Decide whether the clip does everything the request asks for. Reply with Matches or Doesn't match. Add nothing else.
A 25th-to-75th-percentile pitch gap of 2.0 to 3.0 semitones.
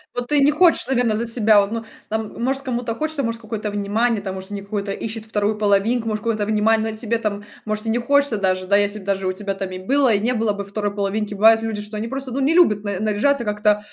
Matches